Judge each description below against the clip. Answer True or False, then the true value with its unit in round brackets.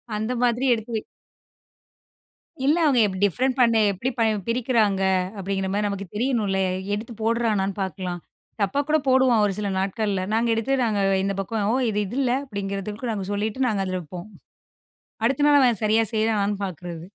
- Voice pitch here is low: False (215 Hz)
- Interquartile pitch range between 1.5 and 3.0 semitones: False (3.4 semitones)